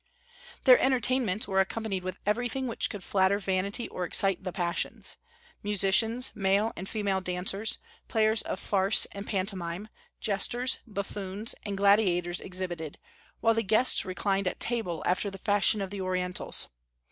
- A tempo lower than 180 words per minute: Yes, average, 145 wpm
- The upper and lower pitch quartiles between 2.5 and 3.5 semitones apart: Yes, average, 2.8 semitones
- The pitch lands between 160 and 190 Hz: No, high, 200 Hz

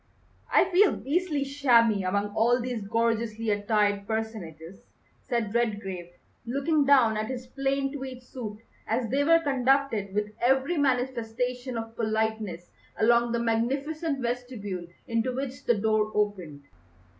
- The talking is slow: Yes, slow, 130 wpm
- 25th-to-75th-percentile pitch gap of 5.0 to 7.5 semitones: No, average, 3.8 semitones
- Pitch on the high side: Yes, high, 235 Hz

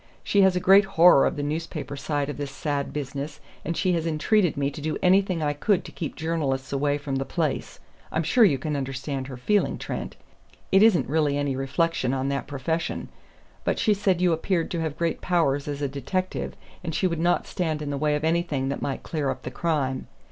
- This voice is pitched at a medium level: Yes, medium, 150 Hz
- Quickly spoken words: Yes, fast, 220 wpm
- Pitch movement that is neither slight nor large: Yes, average, 3.5 semitones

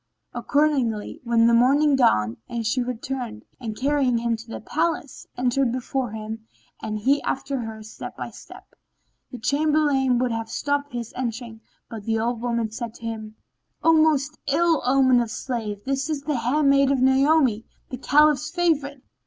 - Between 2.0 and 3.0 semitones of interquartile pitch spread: No, average, 3.8 semitones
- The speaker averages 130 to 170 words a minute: Yes, average, 160 wpm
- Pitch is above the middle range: Yes, very high, 255 Hz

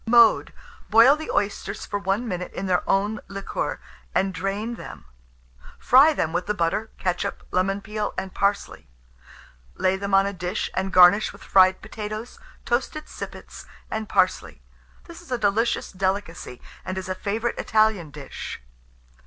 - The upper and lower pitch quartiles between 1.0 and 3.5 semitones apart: Yes, average, 2.8 semitones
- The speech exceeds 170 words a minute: No, average, 155 wpm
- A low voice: No, high, 200 Hz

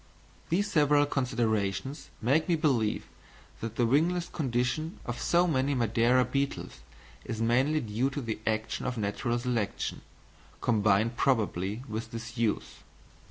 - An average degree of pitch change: Yes, average, 4.1 semitones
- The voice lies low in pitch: Yes, low, 120 Hz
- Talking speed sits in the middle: No, slow, 125 wpm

